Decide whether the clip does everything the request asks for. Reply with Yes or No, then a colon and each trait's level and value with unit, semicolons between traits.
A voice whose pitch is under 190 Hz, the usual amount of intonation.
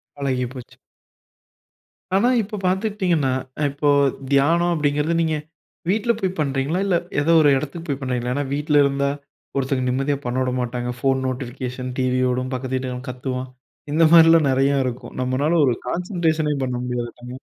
Yes: medium, 140 Hz; average, 3.9 semitones